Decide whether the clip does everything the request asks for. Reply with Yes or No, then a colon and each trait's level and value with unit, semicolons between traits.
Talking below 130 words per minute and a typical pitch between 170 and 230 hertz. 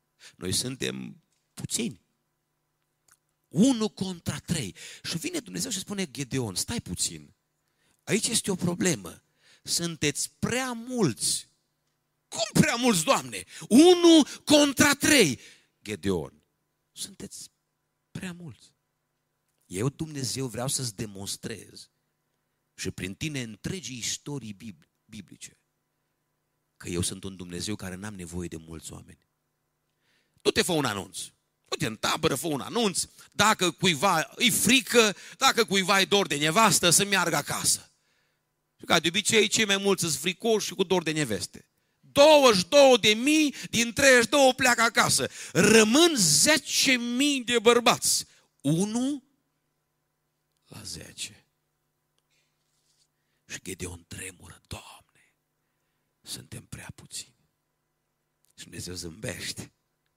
Yes: average, 120 wpm; medium, 185 Hz